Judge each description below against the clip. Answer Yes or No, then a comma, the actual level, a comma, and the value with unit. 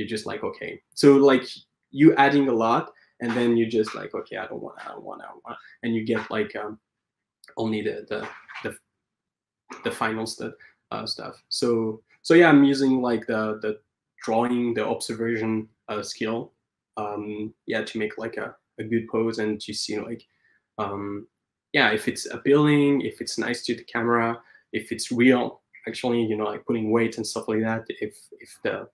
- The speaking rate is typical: Yes, average, 190 wpm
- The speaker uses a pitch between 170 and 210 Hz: No, low, 115 Hz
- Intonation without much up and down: Yes, narrow, 2.0 semitones